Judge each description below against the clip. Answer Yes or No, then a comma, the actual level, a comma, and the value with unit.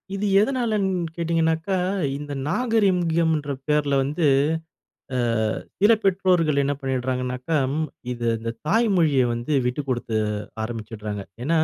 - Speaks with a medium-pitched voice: Yes, medium, 155 Hz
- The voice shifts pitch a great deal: Yes, wide, 6.2 semitones